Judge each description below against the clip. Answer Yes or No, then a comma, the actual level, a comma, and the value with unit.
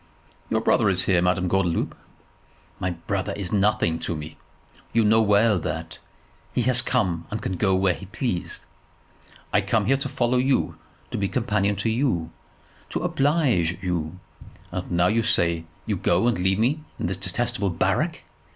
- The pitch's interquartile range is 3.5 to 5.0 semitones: Yes, average, 4.7 semitones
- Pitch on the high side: No, very low, 95 Hz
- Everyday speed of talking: Yes, average, 170 wpm